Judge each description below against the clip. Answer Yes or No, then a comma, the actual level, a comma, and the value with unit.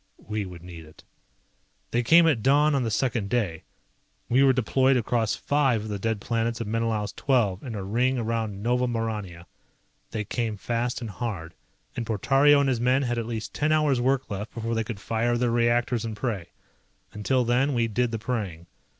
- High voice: No, low, 115 Hz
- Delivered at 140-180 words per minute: No, average, 195 wpm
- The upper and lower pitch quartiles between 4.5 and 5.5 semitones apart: No, average, 3.0 semitones